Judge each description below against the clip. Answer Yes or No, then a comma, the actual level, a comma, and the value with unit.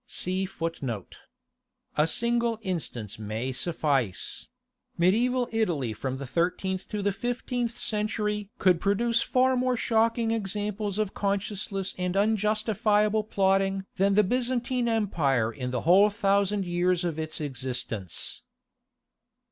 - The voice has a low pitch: No, high, 200 Hz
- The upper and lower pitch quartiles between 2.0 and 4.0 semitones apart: No, average, 4.6 semitones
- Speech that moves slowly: Yes, slow, 115 wpm